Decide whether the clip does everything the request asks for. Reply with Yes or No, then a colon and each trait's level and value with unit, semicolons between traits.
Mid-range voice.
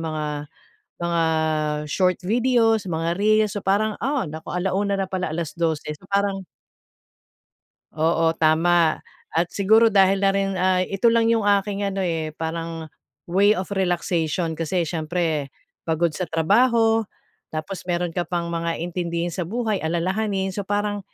Yes: medium, 180 Hz